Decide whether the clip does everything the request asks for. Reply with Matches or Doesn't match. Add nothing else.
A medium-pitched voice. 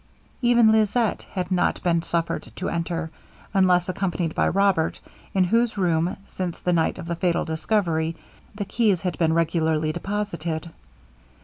Matches